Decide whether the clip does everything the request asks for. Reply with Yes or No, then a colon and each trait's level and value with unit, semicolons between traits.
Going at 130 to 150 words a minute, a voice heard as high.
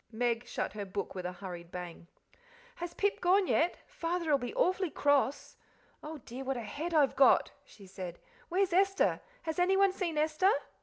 No: average, 170 wpm; very high, 300 Hz